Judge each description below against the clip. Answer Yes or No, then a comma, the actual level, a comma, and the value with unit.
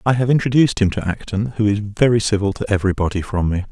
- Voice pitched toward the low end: Yes, low, 105 Hz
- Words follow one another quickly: Yes, fast, 240 wpm